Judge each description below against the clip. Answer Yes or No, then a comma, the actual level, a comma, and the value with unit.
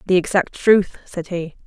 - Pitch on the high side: No, medium, 180 Hz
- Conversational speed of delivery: Yes, average, 180 wpm